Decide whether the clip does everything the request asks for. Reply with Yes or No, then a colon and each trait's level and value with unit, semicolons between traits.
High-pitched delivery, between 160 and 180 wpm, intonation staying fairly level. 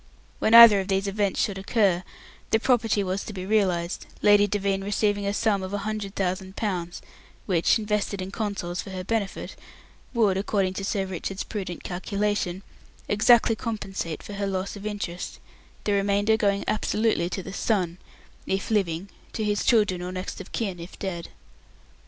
Yes: high, 200 Hz; average, 170 wpm; narrow, 1.9 semitones